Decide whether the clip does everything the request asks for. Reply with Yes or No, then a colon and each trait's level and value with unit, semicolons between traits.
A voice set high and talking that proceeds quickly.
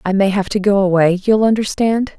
No: high, 200 Hz; average, 190 wpm